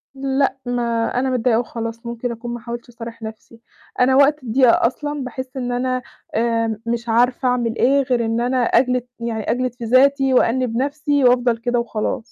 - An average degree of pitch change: No, narrow, 1.9 semitones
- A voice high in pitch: Yes, high, 245 Hz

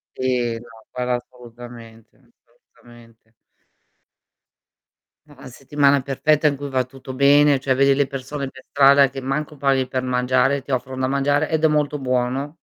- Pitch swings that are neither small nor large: No, narrow, 2.1 semitones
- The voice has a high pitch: No, low, 135 Hz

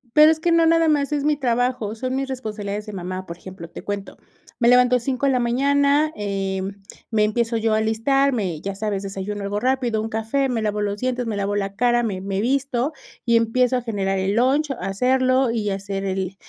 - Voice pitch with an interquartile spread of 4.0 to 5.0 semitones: Yes, average, 4.4 semitones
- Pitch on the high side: Yes, high, 230 Hz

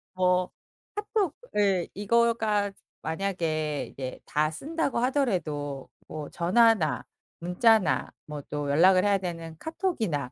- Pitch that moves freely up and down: Yes, wide, 6.6 semitones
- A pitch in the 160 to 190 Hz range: Yes, medium, 185 Hz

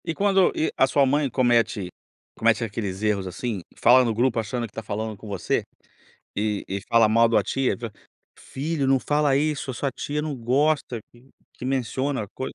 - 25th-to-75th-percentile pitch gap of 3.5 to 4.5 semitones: Yes, average, 3.9 semitones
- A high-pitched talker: No, low, 120 Hz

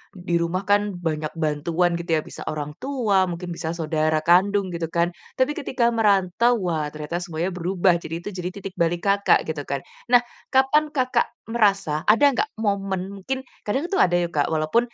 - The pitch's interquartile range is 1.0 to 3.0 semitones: No, average, 3.9 semitones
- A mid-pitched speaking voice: Yes, medium, 180 Hz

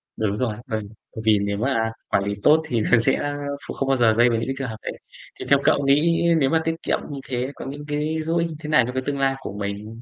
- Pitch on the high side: No, low, 130 Hz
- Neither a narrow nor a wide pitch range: Yes, average, 4.8 semitones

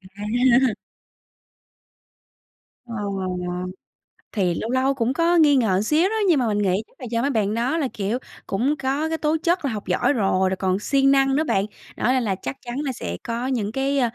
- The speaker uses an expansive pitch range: No, average, 4.9 semitones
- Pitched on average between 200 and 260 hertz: Yes, very high, 250 Hz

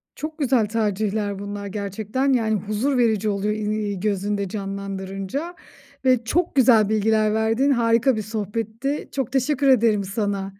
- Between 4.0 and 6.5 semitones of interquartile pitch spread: No, average, 3.5 semitones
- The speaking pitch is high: Yes, high, 215 Hz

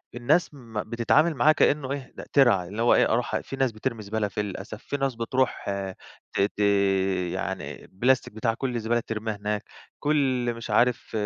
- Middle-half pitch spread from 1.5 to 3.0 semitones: No, average, 3.6 semitones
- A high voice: No, low, 120 Hz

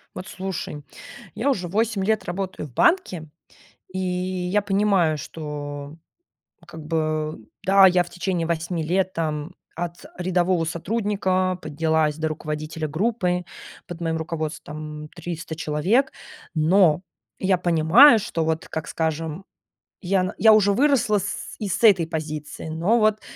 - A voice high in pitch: No, medium, 175 Hz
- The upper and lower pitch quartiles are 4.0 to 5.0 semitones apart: No, average, 3.6 semitones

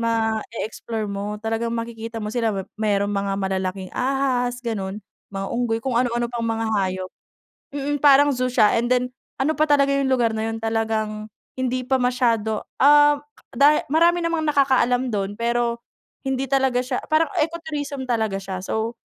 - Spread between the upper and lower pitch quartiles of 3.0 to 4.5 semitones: Yes, average, 3.5 semitones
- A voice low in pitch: No, high, 235 Hz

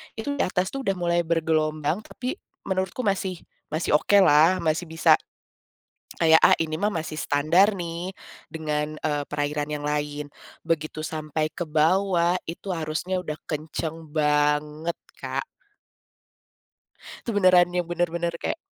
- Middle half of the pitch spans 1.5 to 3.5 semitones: Yes, average, 2.8 semitones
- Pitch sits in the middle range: Yes, medium, 165 Hz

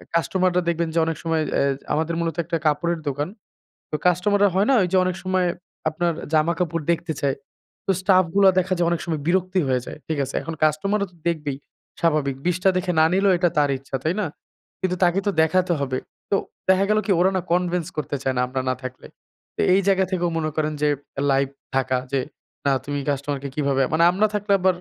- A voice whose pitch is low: No, medium, 170 Hz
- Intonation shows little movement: No, average, 3.7 semitones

